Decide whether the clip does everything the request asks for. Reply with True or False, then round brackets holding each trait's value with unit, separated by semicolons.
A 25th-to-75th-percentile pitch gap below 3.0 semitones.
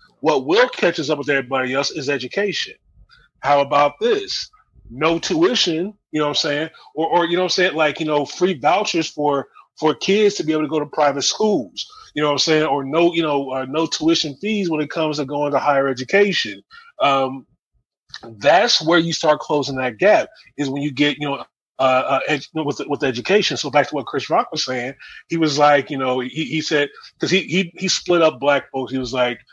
False (3.7 semitones)